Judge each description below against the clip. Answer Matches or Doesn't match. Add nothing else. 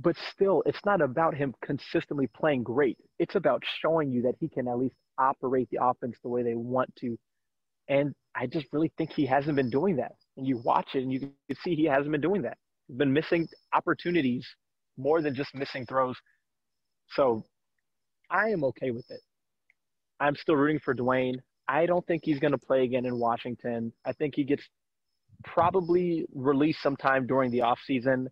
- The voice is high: Doesn't match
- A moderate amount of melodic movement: Matches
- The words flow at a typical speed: Matches